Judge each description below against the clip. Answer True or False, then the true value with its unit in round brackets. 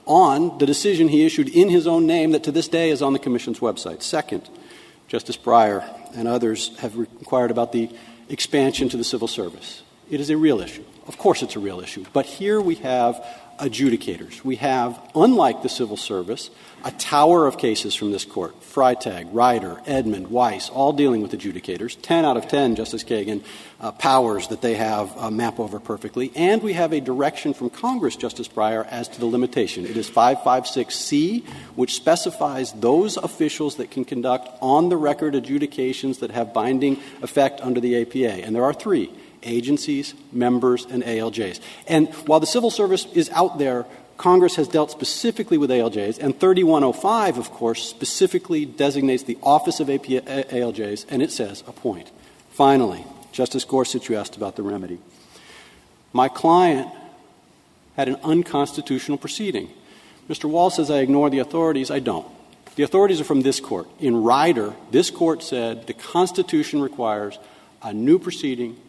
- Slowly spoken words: False (170 wpm)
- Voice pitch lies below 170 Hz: True (135 Hz)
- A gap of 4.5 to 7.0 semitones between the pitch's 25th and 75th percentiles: True (5.6 semitones)